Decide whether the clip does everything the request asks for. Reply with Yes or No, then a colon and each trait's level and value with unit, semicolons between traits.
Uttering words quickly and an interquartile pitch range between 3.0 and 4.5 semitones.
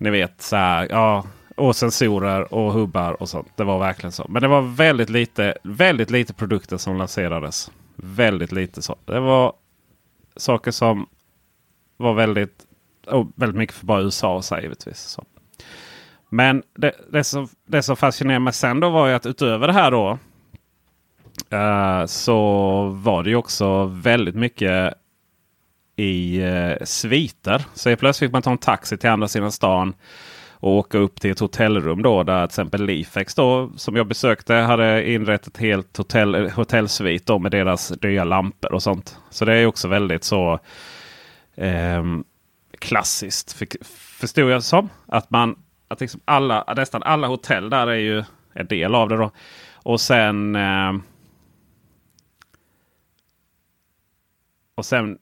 No: average, 155 wpm; average, 4.0 semitones